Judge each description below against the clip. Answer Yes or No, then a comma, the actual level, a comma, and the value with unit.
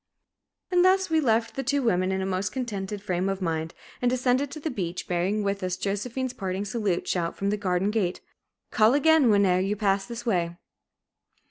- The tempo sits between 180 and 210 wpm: Yes, average, 195 wpm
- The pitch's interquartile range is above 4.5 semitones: Yes, average, 4.9 semitones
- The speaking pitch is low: No, high, 205 Hz